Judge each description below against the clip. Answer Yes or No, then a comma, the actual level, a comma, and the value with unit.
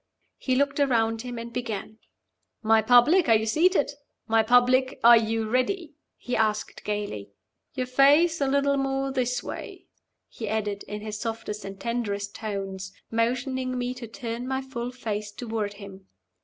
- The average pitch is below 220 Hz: No, high, 235 Hz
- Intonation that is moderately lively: Yes, average, 3.2 semitones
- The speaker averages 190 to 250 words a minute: No, average, 160 wpm